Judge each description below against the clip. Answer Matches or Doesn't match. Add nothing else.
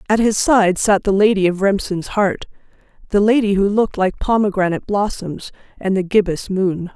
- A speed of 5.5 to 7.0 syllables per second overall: Doesn't match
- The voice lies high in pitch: Matches